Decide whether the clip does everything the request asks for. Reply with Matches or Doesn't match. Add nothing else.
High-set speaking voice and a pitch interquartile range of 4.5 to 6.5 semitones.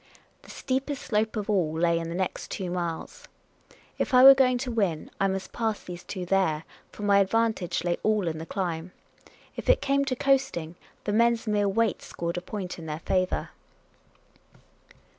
Matches